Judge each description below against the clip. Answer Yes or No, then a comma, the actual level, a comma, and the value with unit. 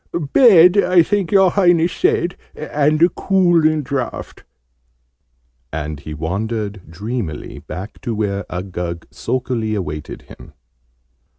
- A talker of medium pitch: No, low, 120 Hz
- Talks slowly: Yes, slow, 110 wpm